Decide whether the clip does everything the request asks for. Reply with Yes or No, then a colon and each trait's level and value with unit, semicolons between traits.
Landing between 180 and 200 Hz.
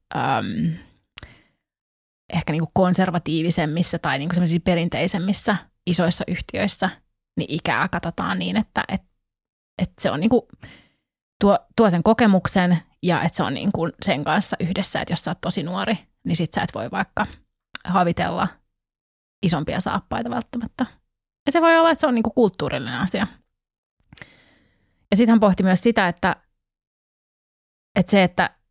Yes: medium, 185 Hz